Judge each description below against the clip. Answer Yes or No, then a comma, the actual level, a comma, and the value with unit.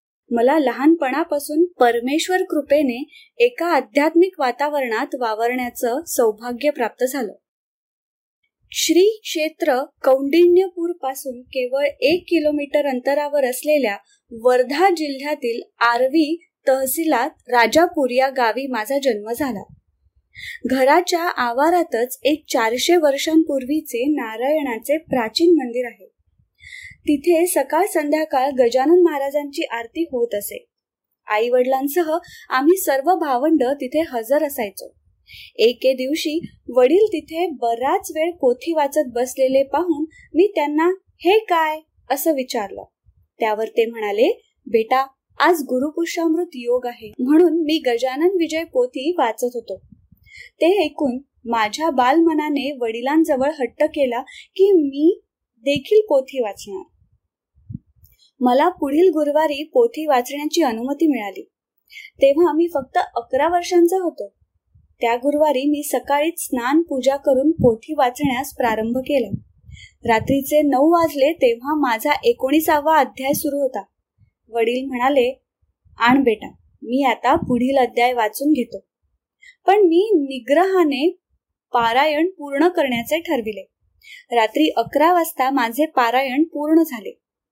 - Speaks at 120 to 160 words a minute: No, average, 105 wpm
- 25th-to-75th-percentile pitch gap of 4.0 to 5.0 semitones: Yes, average, 4.5 semitones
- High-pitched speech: Yes, very high, 290 Hz